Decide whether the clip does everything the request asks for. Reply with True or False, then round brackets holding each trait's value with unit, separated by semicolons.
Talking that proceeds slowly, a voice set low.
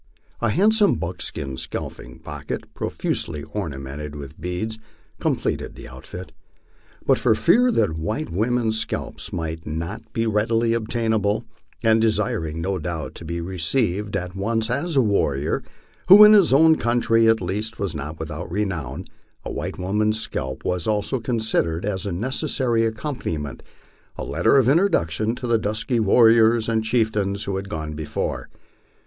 False (155 wpm; 105 Hz)